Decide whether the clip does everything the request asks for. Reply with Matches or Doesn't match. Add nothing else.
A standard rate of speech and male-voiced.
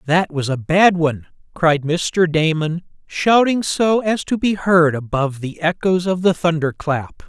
Matches